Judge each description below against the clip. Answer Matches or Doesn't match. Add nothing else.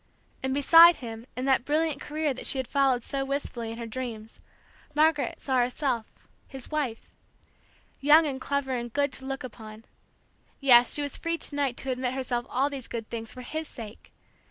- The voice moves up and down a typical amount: Matches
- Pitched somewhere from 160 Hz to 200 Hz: Doesn't match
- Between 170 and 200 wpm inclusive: Matches